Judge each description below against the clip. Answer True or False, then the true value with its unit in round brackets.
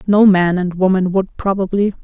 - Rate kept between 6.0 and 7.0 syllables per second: False (4.9 syllables/s)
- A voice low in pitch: False (190 Hz)